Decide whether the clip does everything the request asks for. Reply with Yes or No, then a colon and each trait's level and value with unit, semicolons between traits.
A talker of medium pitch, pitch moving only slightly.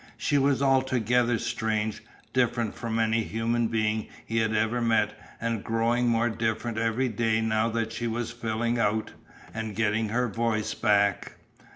No: low, 115 Hz; narrow, 1.3 semitones